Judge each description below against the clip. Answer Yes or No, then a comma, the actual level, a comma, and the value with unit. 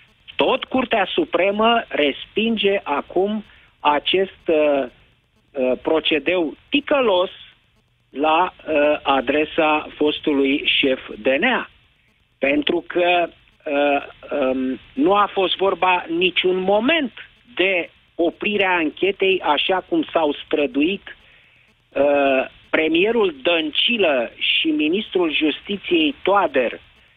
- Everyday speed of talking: No, slow, 90 wpm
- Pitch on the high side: No, medium, 175 Hz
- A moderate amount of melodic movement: No, wide, 8.0 semitones